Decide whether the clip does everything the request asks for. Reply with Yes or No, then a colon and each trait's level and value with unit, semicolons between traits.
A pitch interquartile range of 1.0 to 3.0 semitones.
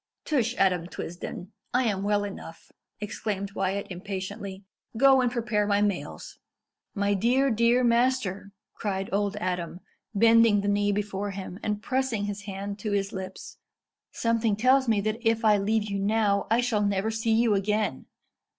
Yes: narrow, 2.5 semitones